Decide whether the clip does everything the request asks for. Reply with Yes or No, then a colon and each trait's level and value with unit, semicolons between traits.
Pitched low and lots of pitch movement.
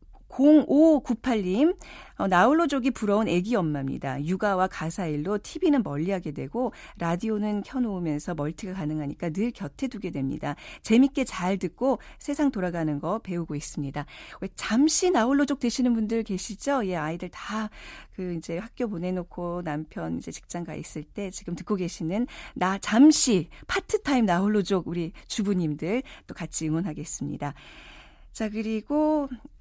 No: high, 195 Hz; wide, 6.6 semitones